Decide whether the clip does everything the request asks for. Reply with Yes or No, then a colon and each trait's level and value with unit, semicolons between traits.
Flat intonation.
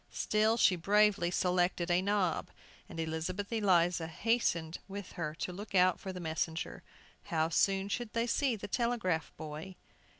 No: average, 3.7 semitones